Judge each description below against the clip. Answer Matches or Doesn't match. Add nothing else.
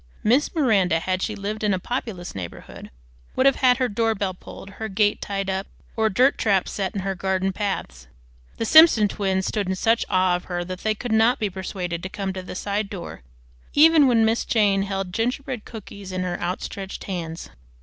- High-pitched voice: Matches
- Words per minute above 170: Matches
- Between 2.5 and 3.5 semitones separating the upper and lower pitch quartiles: Matches